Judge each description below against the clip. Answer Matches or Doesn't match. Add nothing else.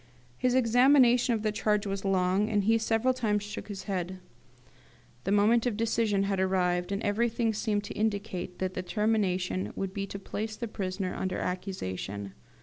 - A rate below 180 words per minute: Matches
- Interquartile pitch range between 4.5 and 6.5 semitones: Doesn't match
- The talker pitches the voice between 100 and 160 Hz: Doesn't match